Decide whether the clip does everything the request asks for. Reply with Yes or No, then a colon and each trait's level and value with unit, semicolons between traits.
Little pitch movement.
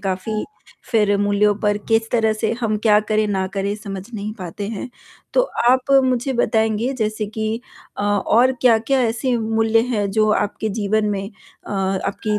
Yes: narrow, 1.7 semitones